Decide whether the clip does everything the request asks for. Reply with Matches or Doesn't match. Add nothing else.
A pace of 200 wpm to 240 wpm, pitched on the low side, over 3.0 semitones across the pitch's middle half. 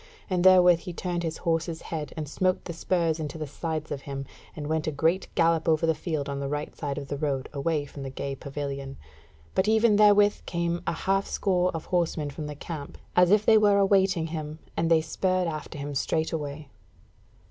Doesn't match